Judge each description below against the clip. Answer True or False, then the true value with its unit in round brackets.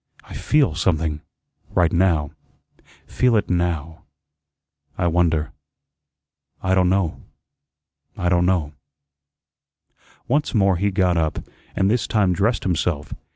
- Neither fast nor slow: False (115 wpm)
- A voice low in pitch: True (90 Hz)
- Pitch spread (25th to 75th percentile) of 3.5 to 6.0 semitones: False (2.9 semitones)